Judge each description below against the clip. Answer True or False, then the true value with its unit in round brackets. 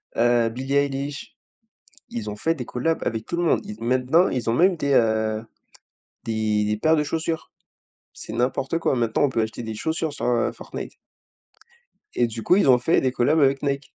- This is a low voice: True (125 Hz)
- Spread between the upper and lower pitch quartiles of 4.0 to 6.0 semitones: True (4.3 semitones)